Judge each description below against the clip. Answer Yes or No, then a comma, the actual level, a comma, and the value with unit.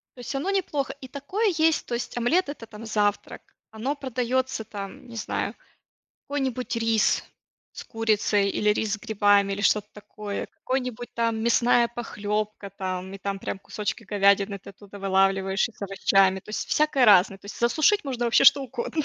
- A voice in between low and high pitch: No, high, 220 Hz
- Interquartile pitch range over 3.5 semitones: Yes, average, 4.2 semitones